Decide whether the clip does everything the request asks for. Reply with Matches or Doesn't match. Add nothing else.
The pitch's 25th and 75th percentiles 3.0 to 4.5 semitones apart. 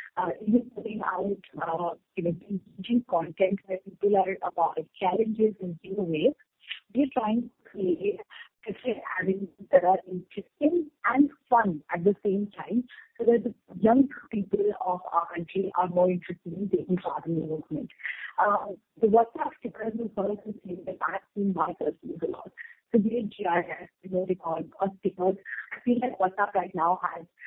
Matches